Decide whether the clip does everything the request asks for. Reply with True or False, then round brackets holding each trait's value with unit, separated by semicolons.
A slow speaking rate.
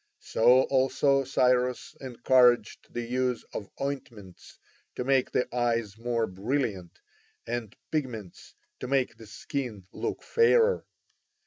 True (115 wpm)